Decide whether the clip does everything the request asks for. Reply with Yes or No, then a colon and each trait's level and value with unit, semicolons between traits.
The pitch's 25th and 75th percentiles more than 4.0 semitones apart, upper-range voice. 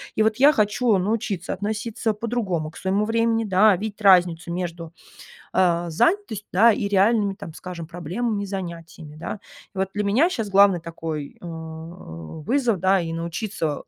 Yes: average, 4.4 semitones; high, 195 Hz